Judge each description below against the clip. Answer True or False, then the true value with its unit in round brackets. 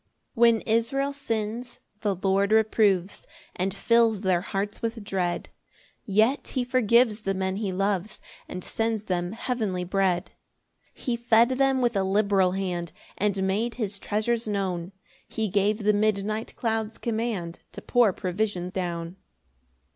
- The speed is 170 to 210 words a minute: False (145 wpm)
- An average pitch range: True (3.1 semitones)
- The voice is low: False (210 Hz)